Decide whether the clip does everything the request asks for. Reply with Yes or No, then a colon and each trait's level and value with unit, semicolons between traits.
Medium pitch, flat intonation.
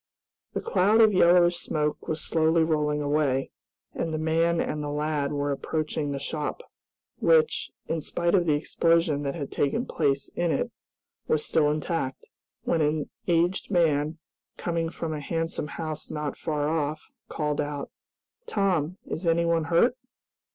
Yes: medium, 155 Hz; narrow, 2.2 semitones